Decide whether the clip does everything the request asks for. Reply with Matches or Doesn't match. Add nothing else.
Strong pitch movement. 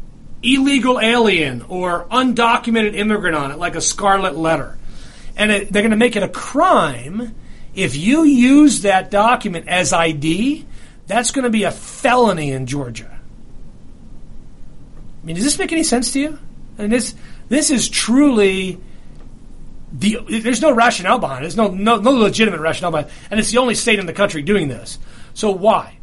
Matches